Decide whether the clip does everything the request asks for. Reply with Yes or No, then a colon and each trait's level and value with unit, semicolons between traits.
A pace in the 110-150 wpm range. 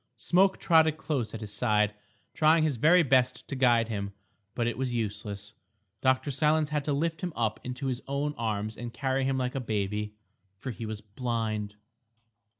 No: average, 180 wpm